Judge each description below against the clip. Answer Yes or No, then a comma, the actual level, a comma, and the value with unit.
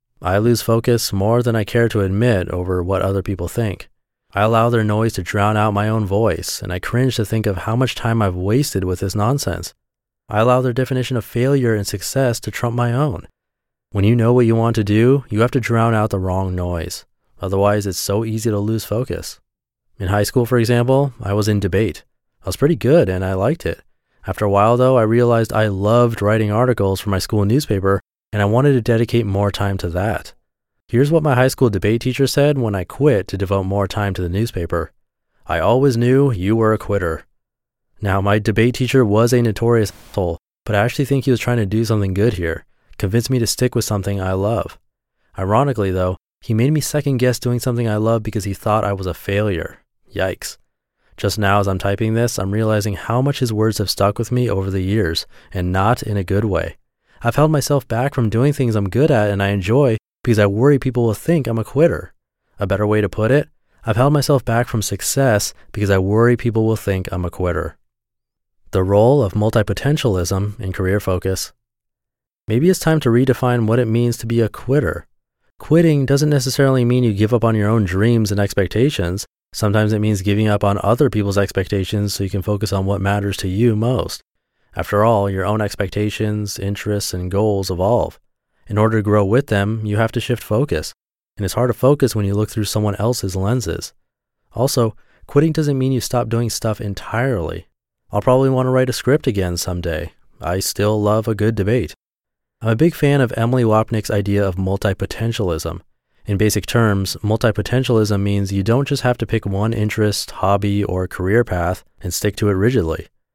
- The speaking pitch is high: No, low, 110 Hz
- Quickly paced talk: Yes, fast, 210 wpm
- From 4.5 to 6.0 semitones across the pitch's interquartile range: No, average, 3.4 semitones